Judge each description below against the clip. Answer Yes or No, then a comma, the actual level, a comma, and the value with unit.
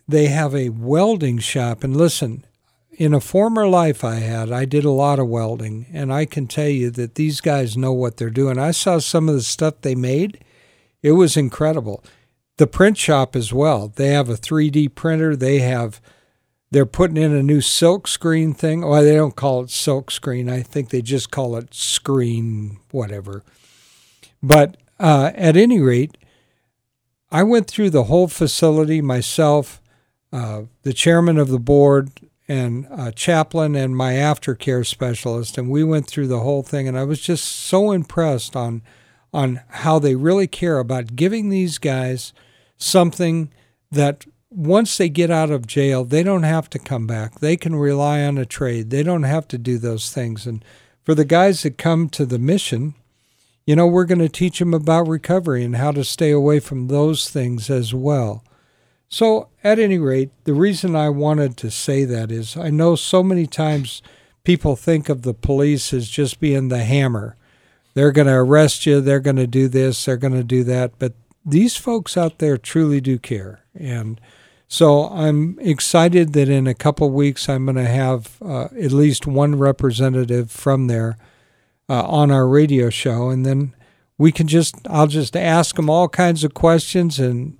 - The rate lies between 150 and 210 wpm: Yes, average, 185 wpm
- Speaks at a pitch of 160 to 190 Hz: No, medium, 140 Hz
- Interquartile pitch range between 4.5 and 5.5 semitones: No, average, 3.9 semitones